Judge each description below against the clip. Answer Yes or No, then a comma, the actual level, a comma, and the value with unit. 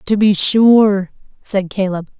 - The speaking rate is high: No, slow, 135 wpm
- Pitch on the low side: No, high, 200 Hz